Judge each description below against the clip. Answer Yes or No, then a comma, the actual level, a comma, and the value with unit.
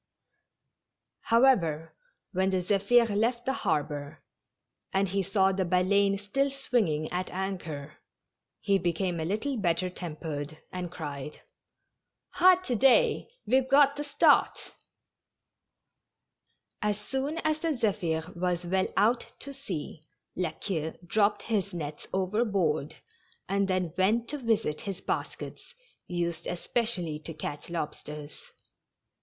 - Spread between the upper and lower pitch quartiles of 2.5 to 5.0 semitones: No, wide, 5.6 semitones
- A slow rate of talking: Yes, slow, 125 wpm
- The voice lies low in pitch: No, high, 190 Hz